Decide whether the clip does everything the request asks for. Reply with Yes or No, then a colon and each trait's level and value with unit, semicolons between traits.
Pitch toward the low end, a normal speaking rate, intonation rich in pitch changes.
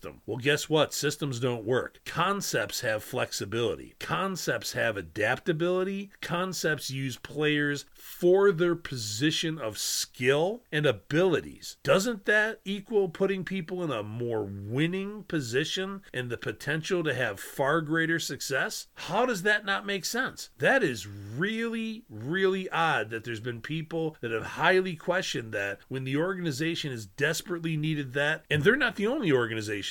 No: medium, 155 Hz; average, 145 wpm; wide, 6.4 semitones